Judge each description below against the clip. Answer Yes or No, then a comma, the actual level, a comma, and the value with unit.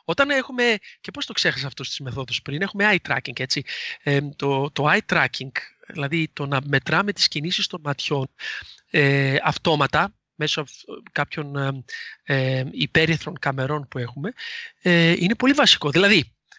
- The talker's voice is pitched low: No, medium, 150 Hz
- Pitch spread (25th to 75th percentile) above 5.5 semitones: Yes, wide, 5.9 semitones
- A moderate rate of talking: Yes, average, 150 wpm